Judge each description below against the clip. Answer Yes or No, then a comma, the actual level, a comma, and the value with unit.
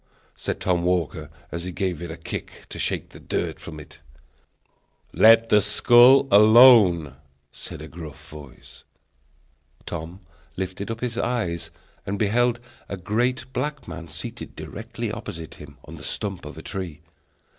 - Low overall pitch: Yes, very low, 95 Hz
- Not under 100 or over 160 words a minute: Yes, average, 150 wpm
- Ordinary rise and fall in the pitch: No, wide, 5.7 semitones